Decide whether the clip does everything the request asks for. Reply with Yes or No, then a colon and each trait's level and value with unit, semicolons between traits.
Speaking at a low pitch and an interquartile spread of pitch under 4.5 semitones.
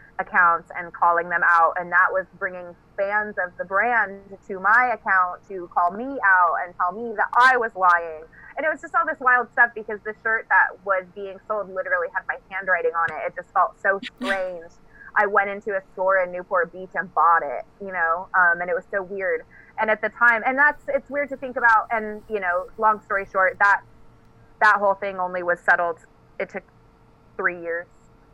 No: high, 195 Hz; average, 3.8 semitones